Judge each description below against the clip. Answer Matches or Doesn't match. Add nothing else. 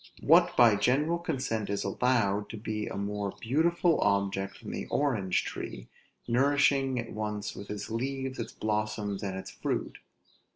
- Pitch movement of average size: Matches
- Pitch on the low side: Matches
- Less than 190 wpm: Matches